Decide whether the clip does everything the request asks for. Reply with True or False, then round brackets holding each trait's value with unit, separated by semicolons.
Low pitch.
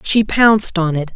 False (190 Hz)